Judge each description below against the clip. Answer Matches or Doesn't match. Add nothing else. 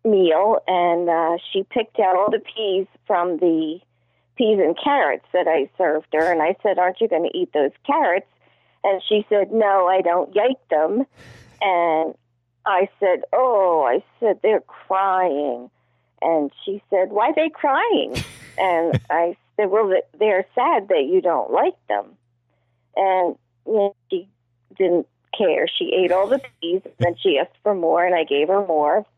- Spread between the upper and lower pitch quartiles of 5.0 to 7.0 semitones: Matches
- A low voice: Doesn't match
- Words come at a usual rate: Matches